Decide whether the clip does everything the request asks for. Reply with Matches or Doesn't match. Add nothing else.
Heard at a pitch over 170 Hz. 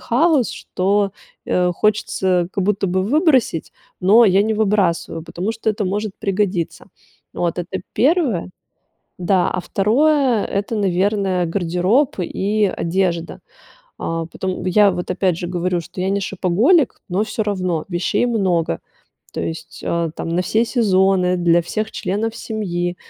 Matches